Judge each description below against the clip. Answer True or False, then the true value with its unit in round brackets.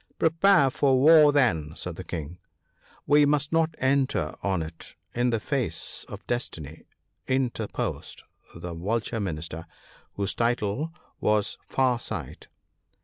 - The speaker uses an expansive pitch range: True (8.2 semitones)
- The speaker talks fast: False (145 wpm)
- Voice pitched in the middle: False (120 Hz)